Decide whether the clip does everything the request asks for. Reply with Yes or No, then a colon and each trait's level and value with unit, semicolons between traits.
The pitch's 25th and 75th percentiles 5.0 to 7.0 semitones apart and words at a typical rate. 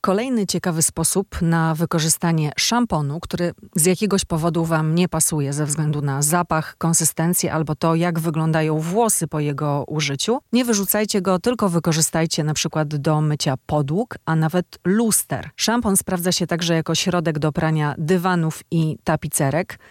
No: average, 2.8 semitones; average, 150 wpm